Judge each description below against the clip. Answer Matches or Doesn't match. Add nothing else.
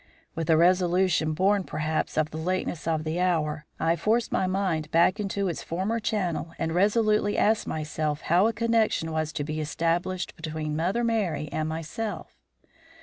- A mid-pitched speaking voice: Matches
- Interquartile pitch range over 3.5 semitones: Matches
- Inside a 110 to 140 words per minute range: Doesn't match